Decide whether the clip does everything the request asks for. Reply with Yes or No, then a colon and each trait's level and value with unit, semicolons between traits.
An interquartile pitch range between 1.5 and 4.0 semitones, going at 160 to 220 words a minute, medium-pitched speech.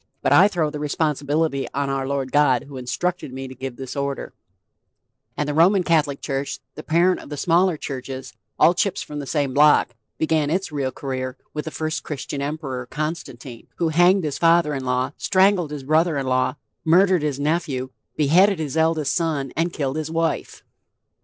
Yes: average, 3.3 semitones; average, 185 wpm; medium, 150 Hz